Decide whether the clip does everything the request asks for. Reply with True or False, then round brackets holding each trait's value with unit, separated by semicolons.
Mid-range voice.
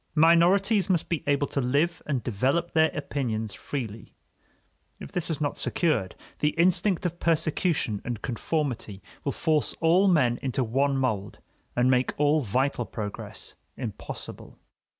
True (145 Hz)